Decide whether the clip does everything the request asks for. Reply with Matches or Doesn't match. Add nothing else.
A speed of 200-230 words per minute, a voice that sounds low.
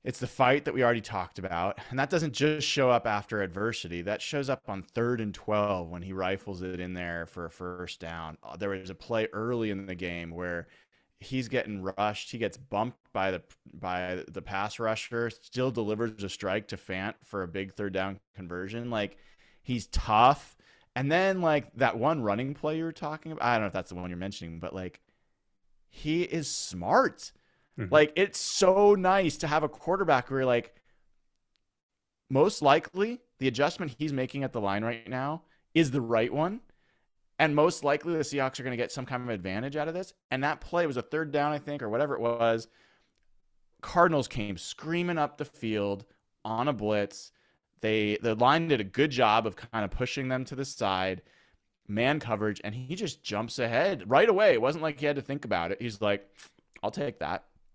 Matches